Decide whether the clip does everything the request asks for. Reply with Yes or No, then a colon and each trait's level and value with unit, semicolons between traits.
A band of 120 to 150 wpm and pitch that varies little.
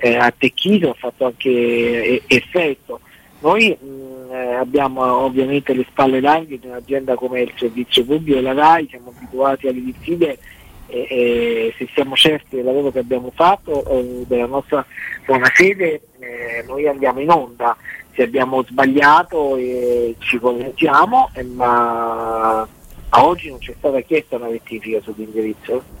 Yes: average, 145 wpm; narrow, 2.3 semitones